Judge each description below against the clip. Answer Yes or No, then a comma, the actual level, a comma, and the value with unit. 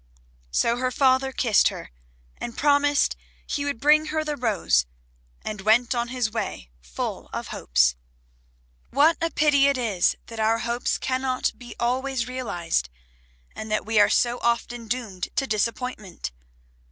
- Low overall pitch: No, high, 240 Hz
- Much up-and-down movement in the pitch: No, average, 3.7 semitones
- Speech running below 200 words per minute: Yes, average, 150 wpm